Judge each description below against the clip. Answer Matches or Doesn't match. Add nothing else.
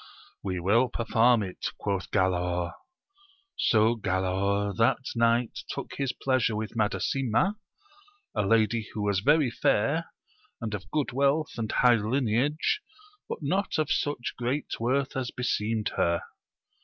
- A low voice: Matches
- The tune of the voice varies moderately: Matches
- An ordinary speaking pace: Doesn't match